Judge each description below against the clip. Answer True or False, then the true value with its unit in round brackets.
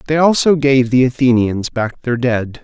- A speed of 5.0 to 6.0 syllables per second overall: False (4.6 syllables/s)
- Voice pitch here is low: True (130 Hz)